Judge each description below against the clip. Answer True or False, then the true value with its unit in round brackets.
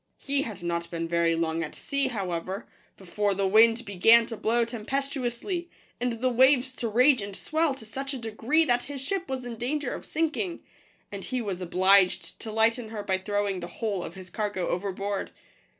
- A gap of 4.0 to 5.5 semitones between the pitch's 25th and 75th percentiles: True (5.1 semitones)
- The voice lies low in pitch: False (225 Hz)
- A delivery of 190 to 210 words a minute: True (195 wpm)